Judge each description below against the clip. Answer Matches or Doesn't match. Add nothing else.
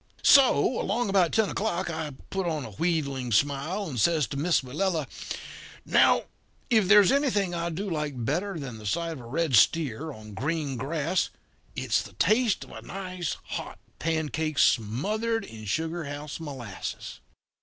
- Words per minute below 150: Doesn't match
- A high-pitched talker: Doesn't match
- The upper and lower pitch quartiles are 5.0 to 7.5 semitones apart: Matches